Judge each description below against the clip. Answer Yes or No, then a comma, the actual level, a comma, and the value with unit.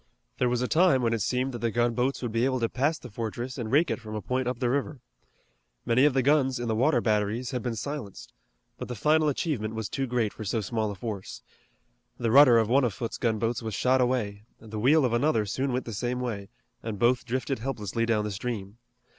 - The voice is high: No, low, 120 Hz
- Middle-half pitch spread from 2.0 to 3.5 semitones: Yes, average, 2.8 semitones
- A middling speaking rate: No, fast, 235 wpm